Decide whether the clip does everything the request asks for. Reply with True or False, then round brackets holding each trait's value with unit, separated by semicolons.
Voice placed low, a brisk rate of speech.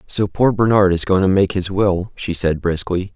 True (95 Hz; 230 wpm)